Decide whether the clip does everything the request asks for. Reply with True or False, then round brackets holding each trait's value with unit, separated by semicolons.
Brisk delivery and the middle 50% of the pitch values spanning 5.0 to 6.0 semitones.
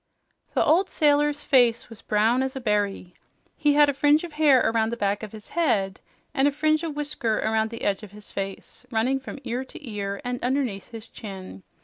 True (210 wpm; 5.6 semitones)